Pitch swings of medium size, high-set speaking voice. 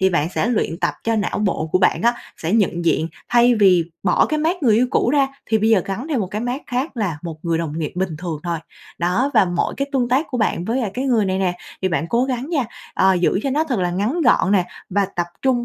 No: wide, 5.9 semitones; high, 210 Hz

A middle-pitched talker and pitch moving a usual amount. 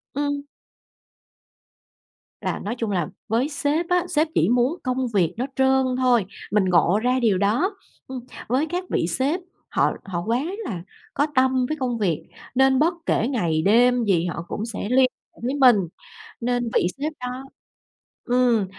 No: very high, 250 Hz; average, 4.4 semitones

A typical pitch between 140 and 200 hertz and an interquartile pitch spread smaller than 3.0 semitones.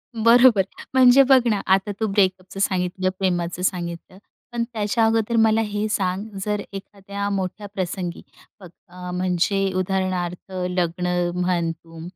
Yes: high, 190 Hz; narrow, 2.6 semitones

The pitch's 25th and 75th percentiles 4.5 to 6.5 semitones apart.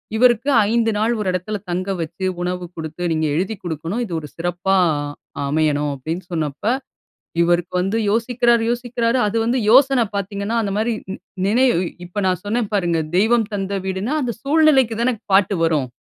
Yes: average, 5.1 semitones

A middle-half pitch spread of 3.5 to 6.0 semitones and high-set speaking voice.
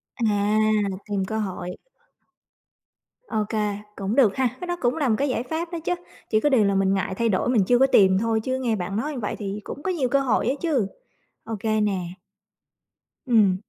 Yes: average, 4.4 semitones; high, 220 Hz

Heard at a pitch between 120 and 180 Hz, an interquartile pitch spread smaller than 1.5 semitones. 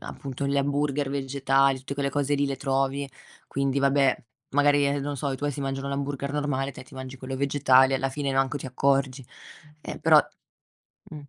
Yes: medium, 140 Hz; narrow, 1.0 semitones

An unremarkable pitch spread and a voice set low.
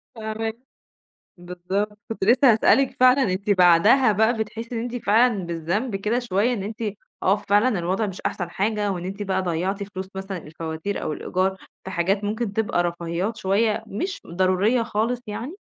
No: average, 3.3 semitones; high, 205 Hz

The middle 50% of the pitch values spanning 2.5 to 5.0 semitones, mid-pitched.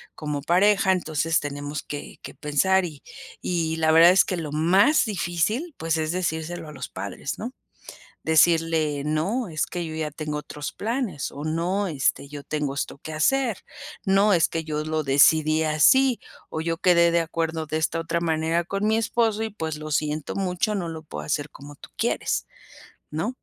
Yes: average, 3.3 semitones; medium, 160 Hz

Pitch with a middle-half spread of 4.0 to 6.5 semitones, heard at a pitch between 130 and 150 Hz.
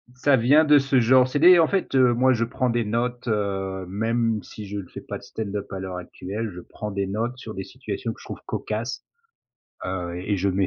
No: average, 4.4 semitones; low, 115 Hz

